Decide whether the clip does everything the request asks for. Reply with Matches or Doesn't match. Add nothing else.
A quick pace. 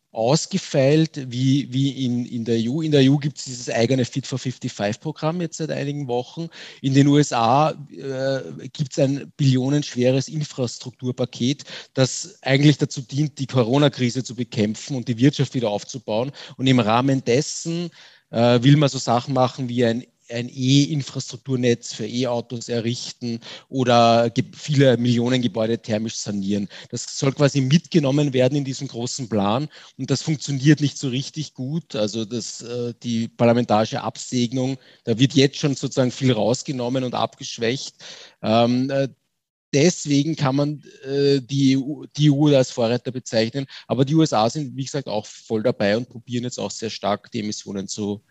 Doesn't match